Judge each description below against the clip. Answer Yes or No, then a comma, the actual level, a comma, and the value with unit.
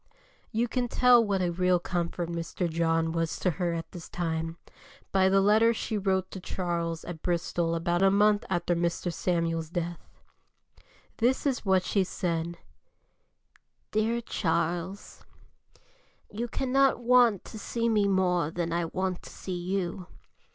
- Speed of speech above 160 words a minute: No, average, 150 wpm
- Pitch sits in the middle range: Yes, medium, 180 Hz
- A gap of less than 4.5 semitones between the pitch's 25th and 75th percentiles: Yes, average, 3.5 semitones